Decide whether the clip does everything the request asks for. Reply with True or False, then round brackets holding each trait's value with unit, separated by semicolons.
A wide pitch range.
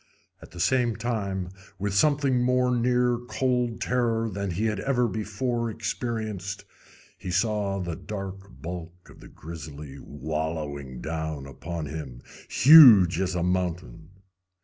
True (6.1 semitones)